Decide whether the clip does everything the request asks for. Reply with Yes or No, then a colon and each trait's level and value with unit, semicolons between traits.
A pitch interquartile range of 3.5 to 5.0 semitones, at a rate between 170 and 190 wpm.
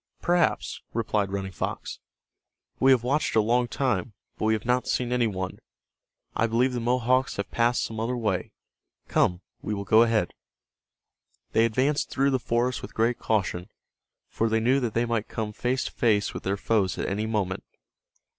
No: average, 2.8 semitones; average, 180 wpm